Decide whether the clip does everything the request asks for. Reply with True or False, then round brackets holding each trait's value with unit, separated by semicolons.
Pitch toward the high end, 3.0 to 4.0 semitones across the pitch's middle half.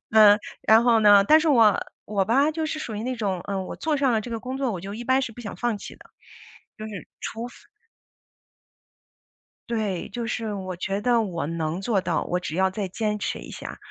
True (215 Hz; 3.7 semitones)